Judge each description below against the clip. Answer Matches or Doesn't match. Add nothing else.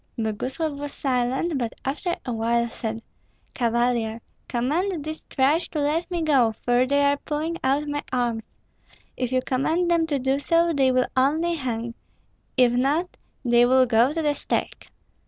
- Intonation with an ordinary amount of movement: Matches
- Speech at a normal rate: Matches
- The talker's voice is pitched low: Doesn't match